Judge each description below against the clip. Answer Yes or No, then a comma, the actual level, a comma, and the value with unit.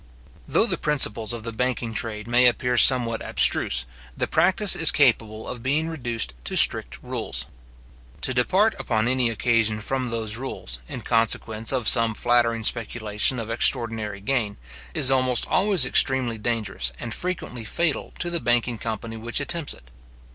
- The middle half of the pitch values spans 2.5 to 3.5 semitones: Yes, average, 2.8 semitones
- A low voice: Yes, low, 120 Hz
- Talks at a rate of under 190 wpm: Yes, average, 155 wpm